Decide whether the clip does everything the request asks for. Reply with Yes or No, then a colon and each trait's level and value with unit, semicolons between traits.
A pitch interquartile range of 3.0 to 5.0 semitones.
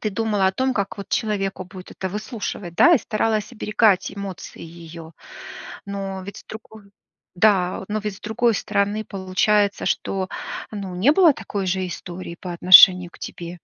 No: narrow, 2.6 semitones